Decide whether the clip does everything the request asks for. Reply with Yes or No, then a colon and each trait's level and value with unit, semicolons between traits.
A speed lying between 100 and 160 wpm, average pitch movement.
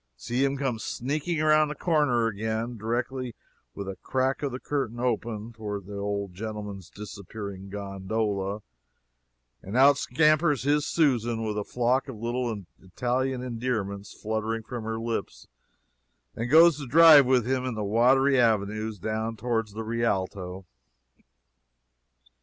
Yes: average, 140 wpm; average, 3.9 semitones